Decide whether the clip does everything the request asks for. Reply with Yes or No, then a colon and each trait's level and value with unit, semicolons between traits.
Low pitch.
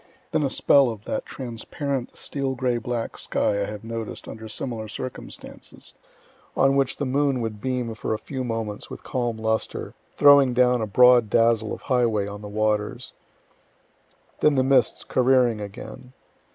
Yes: low, 120 Hz